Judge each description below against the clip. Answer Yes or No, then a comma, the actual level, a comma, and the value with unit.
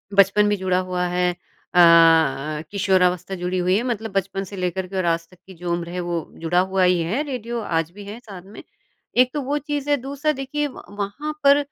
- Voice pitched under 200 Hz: Yes, high, 190 Hz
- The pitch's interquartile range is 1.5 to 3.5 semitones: No, average, 5.1 semitones